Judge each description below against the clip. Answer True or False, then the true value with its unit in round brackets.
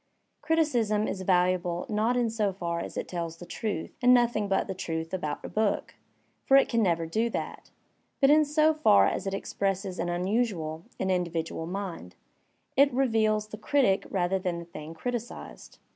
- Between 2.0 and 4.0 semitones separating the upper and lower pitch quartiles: False (5.1 semitones)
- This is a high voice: True (195 Hz)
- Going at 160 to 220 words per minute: True (180 wpm)